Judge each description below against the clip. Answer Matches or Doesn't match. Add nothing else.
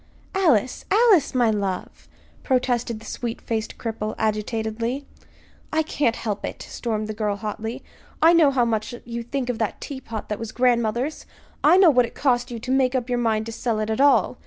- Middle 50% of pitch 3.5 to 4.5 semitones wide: Doesn't match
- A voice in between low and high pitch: Doesn't match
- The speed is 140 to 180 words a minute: Doesn't match